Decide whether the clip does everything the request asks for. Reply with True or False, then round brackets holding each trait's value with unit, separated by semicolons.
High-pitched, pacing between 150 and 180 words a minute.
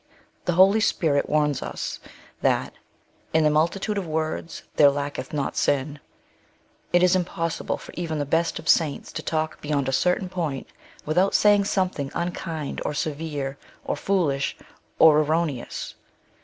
False (160 Hz; 155 wpm)